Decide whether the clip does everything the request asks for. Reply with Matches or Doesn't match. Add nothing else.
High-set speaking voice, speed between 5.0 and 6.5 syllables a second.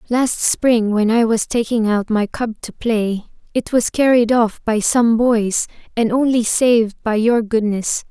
Doesn't match